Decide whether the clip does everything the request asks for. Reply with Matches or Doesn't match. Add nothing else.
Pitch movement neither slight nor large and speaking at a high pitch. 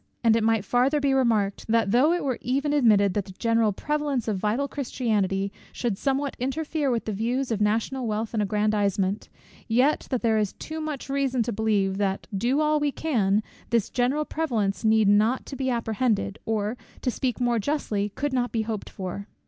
Matches